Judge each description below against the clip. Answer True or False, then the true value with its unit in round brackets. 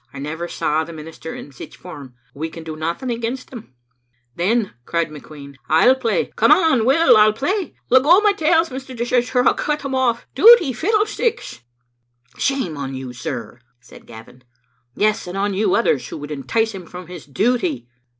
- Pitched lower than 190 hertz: False (215 Hz)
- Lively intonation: True (9.0 semitones)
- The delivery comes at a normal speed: True (180 wpm)